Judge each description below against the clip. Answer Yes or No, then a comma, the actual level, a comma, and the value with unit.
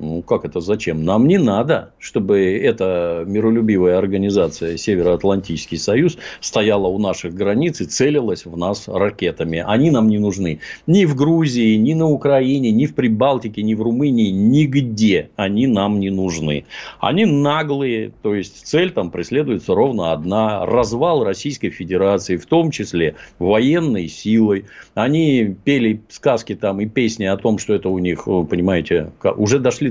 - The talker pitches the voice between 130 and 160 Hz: No, low, 105 Hz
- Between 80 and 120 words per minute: No, average, 150 wpm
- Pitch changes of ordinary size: No, wide, 6.4 semitones